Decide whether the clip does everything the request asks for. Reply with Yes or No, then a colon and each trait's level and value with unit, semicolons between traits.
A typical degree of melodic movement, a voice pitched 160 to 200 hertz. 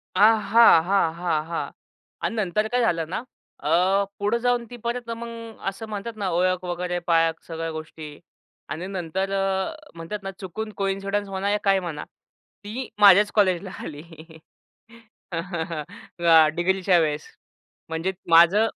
Yes: average, 3.8 semitones; high, 190 Hz